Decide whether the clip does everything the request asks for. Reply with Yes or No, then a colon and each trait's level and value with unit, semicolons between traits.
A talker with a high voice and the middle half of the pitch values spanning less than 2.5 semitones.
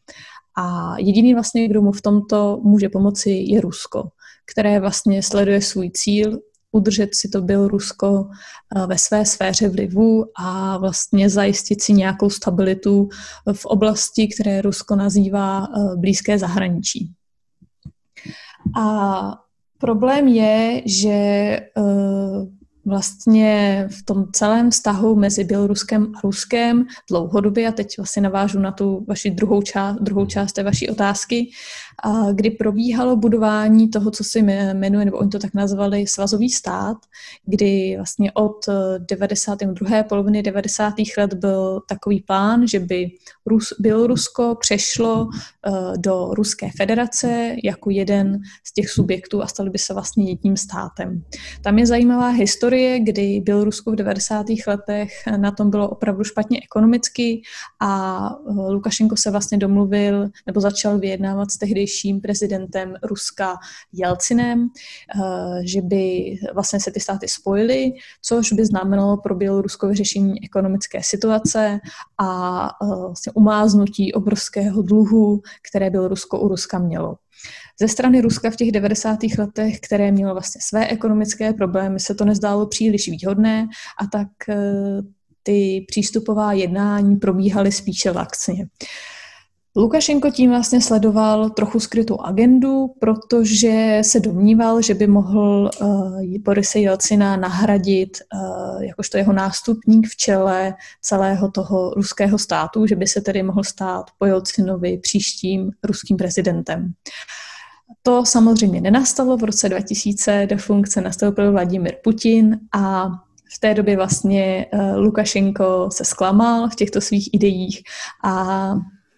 Yes: high, 205 Hz; narrow, 1.8 semitones